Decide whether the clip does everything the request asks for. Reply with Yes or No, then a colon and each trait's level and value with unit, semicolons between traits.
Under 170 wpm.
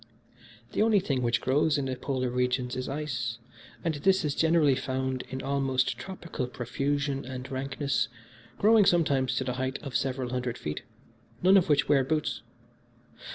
Yes: average, 160 wpm